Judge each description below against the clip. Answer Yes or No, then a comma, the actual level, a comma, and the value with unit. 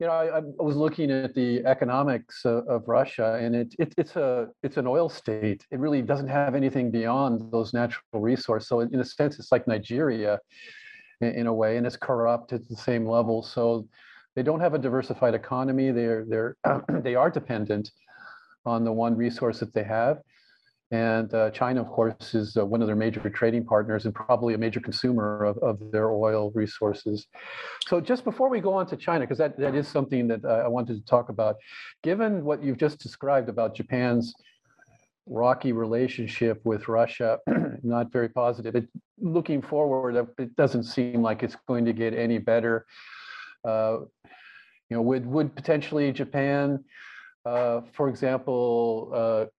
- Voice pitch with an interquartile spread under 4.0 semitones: Yes, average, 3.3 semitones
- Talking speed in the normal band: Yes, average, 180 wpm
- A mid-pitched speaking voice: No, low, 120 Hz